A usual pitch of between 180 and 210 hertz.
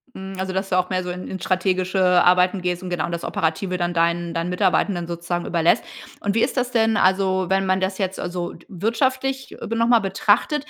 Yes: medium, 185 Hz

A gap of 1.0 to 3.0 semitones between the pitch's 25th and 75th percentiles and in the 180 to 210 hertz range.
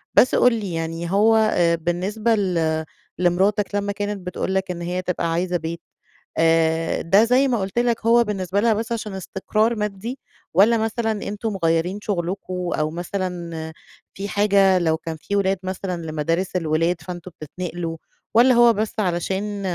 No: average, 3.6 semitones; high, 190 Hz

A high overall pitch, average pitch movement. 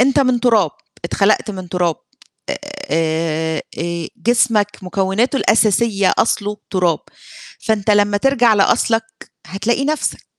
Yes: high, 205 Hz; average, 4.4 semitones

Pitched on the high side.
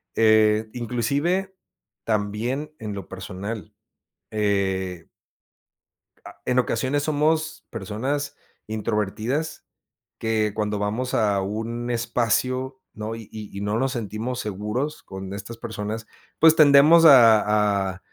No: low, 110 Hz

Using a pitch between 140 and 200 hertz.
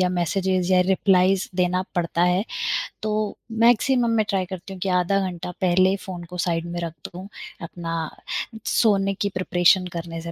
Yes: medium, 185 Hz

